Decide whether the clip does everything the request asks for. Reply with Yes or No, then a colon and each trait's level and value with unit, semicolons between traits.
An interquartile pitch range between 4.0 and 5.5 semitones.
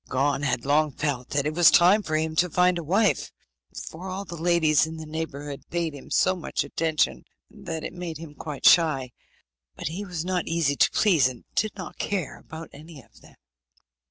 No: average, 3.2 semitones